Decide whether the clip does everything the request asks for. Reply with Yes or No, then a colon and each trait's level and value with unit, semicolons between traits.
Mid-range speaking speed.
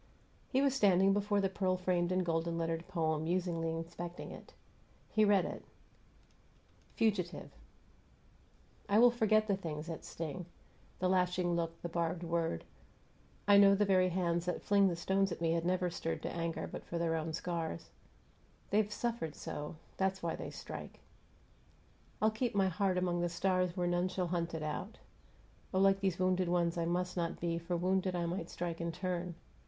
Yes: average, 180 wpm